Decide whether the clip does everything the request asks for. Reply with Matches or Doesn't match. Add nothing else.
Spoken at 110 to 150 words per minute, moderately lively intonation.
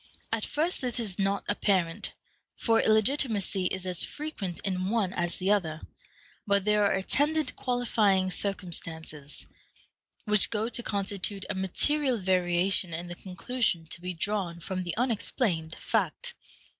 Matches